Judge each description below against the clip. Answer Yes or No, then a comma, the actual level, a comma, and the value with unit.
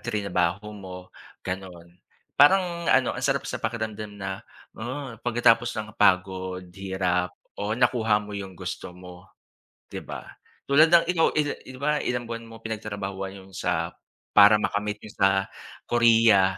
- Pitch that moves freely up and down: No, average, 3.8 semitones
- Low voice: Yes, low, 105 Hz